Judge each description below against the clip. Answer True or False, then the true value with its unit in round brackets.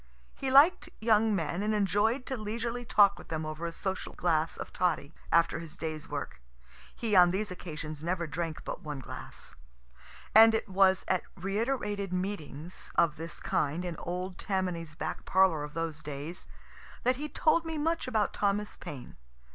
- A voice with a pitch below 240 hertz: True (185 Hz)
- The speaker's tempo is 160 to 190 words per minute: True (170 wpm)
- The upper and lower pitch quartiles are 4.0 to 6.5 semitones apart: True (4.7 semitones)